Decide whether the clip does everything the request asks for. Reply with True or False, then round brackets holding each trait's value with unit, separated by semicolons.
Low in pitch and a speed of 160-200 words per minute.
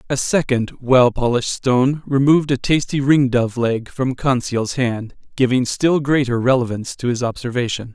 False (130 Hz; 150 wpm)